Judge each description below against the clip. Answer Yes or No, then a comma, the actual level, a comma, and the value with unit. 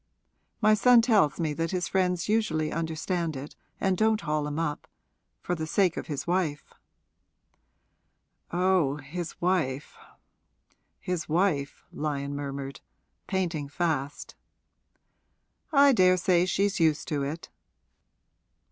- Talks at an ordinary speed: No, slow, 115 wpm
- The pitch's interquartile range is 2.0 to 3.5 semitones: No, average, 4.0 semitones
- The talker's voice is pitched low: No, medium, 165 Hz